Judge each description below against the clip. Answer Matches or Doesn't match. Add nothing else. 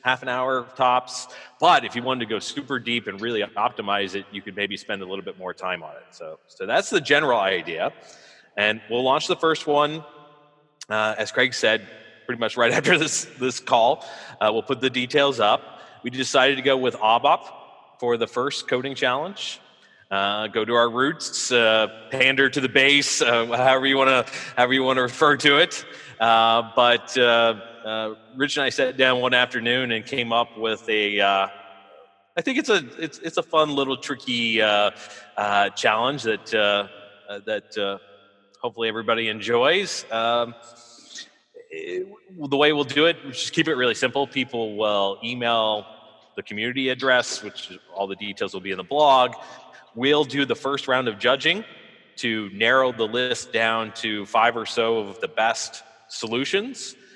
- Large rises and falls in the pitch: Doesn't match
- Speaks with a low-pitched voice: Matches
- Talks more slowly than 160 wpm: Doesn't match